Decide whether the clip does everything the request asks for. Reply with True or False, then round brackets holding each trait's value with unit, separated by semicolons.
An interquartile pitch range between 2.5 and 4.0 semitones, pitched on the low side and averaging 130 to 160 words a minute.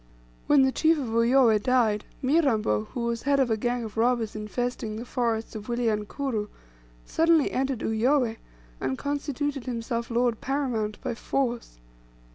False (3.4 semitones; 240 Hz; 145 wpm)